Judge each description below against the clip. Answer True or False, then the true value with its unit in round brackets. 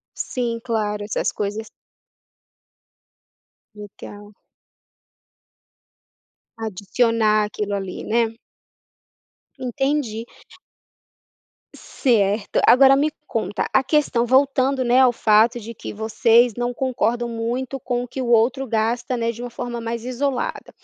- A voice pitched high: True (235 Hz)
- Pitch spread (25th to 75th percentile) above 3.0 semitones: False (2.7 semitones)